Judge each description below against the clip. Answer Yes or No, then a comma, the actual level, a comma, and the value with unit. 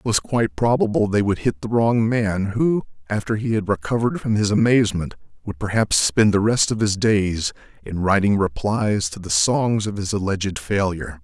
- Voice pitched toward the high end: No, low, 105 Hz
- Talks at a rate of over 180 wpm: Yes, average, 190 wpm